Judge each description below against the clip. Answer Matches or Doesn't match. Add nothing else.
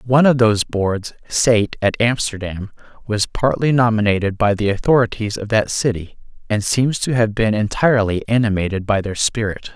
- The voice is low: Matches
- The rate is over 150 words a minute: Matches